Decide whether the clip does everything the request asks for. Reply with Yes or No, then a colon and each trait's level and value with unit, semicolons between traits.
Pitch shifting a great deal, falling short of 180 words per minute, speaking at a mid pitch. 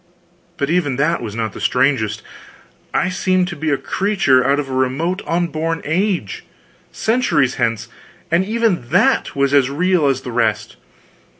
Yes: wide, 5.8 semitones; average, 160 wpm; medium, 145 Hz